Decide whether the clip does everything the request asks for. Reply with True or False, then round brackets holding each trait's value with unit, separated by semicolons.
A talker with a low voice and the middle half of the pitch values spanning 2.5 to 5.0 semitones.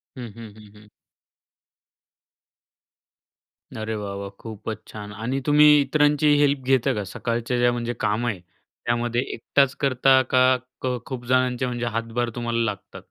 True (120 Hz; 2.8 semitones)